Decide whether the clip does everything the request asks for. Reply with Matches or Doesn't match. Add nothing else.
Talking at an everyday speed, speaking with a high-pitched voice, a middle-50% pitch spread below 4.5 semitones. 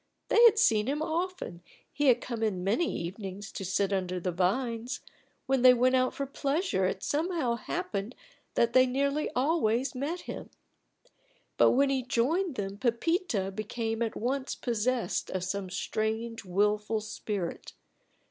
Doesn't match